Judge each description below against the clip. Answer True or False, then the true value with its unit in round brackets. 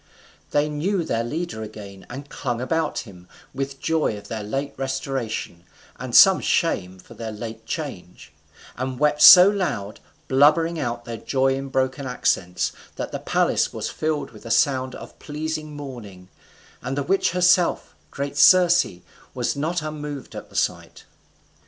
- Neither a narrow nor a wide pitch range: True (4.9 semitones)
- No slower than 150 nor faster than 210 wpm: True (155 wpm)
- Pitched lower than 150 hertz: True (135 Hz)